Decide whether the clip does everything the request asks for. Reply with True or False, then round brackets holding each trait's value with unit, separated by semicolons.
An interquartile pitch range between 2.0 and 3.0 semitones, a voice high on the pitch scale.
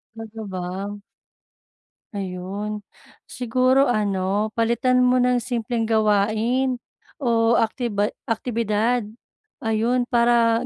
True (2.6 semitones; 225 Hz)